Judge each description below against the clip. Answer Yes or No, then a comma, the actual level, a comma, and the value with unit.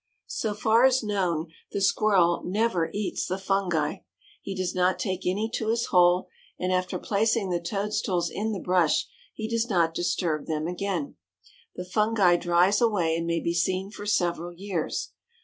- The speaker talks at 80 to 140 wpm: No, average, 165 wpm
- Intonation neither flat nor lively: Yes, average, 3.2 semitones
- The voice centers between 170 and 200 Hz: Yes, medium, 185 Hz